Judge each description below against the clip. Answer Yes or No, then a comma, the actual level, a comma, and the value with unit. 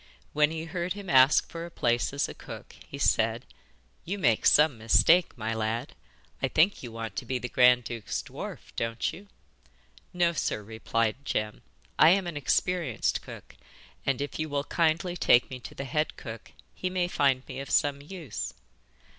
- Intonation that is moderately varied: No, wide, 6.1 semitones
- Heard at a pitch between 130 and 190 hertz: Yes, medium, 140 Hz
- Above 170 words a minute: Yes, average, 180 wpm